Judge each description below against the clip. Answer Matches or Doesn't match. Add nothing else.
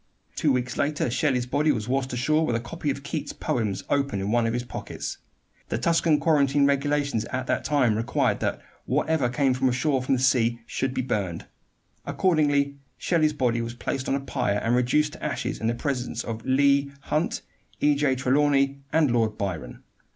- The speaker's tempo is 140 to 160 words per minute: Doesn't match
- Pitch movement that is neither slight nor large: Matches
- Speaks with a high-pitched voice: Doesn't match